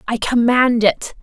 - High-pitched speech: Yes, high, 235 Hz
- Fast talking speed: No, average, 145 wpm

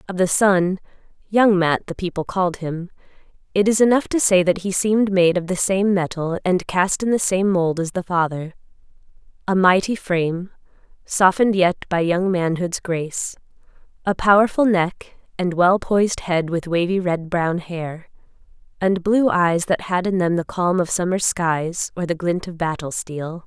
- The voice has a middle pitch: Yes, medium, 180 Hz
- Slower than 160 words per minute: No, average, 180 wpm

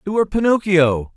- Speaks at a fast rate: No, average, 155 wpm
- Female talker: No, male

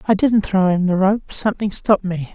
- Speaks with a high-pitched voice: Yes, high, 195 Hz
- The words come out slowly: No, fast, 230 wpm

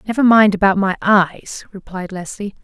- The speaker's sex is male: No, female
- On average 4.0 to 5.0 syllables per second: Yes, 4.7 syllables/s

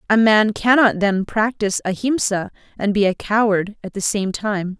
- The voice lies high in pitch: Yes, high, 210 Hz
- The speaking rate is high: No, average, 175 wpm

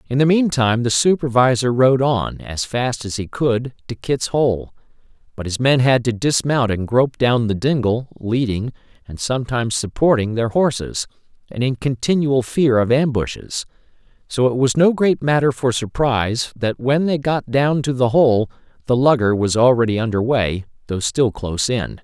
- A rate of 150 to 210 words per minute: Yes, average, 175 wpm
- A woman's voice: No, male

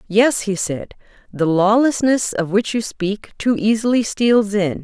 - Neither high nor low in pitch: No, high, 210 Hz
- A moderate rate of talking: Yes, average, 160 wpm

